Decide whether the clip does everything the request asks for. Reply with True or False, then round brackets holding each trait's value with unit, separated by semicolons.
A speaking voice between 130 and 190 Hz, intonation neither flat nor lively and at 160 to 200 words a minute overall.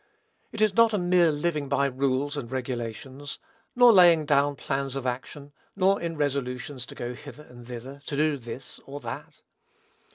True (140 Hz; 3.2 semitones; 170 wpm)